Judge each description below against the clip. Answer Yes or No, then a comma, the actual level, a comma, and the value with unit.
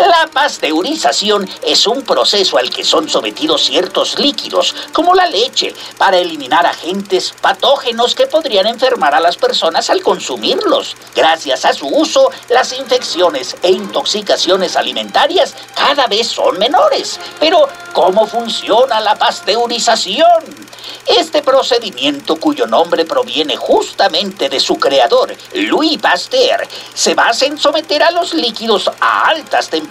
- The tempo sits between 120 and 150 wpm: Yes, average, 130 wpm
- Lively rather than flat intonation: Yes, wide, 6.1 semitones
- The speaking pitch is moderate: No, very high, 275 Hz